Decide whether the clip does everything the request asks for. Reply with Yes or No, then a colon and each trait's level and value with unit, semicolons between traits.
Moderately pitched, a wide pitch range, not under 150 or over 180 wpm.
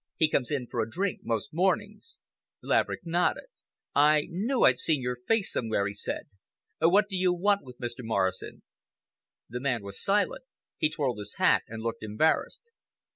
Yes: medium, 145 Hz; wide, 8.4 semitones; average, 170 wpm